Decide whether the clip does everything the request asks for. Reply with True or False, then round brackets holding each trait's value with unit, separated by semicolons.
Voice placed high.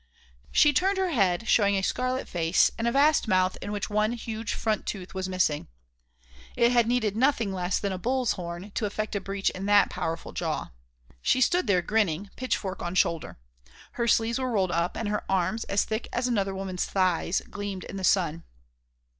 True (205 Hz)